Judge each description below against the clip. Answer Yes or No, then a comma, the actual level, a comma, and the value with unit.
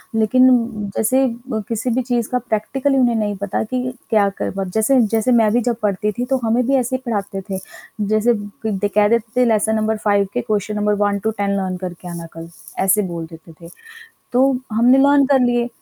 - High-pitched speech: Yes, high, 220 Hz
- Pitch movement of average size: Yes, average, 3.2 semitones